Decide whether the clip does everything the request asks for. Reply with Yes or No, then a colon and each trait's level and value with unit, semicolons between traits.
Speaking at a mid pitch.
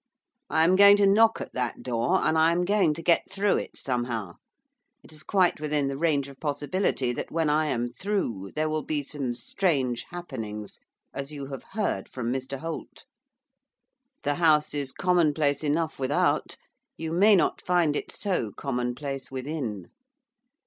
Yes: medium, 150 Hz